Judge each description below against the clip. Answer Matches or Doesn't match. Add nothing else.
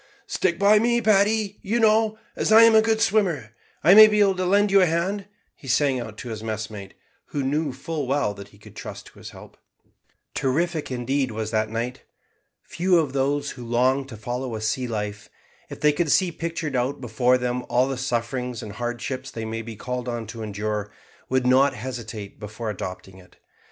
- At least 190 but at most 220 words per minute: Matches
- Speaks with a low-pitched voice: Matches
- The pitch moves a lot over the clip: Matches